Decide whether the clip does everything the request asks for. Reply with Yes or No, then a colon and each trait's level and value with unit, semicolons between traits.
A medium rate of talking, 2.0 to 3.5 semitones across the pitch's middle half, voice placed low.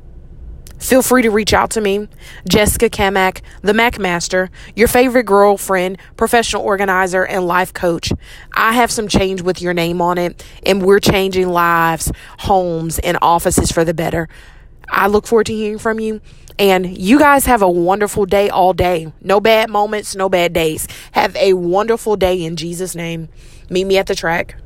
No: average, 175 wpm; average, 3.2 semitones; high, 190 Hz